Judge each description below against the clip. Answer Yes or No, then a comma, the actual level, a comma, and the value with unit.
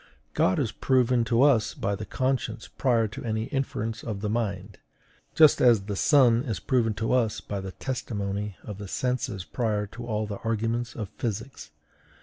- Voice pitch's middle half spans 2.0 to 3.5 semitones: Yes, average, 2.9 semitones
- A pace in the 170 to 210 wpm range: Yes, average, 175 wpm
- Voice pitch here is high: No, low, 115 Hz